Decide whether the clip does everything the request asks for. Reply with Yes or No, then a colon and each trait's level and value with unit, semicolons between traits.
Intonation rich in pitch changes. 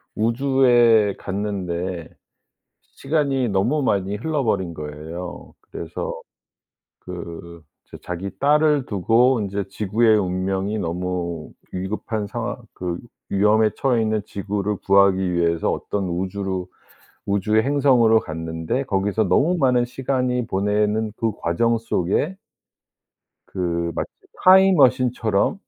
No: average, 4.9 semitones